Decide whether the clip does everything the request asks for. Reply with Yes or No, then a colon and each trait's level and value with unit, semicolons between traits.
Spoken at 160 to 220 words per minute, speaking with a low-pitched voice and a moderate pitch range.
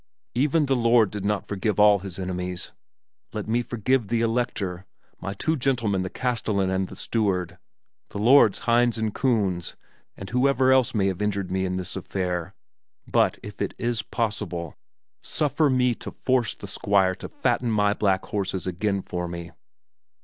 Yes: average, 165 wpm; low, 105 Hz; average, 4.2 semitones